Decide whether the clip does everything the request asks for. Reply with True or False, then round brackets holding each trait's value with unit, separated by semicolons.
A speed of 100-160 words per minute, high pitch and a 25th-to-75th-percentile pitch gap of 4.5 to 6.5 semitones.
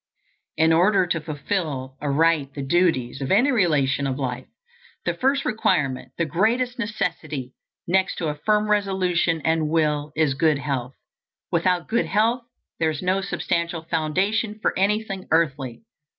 False (145 wpm; 165 Hz; 5.1 semitones)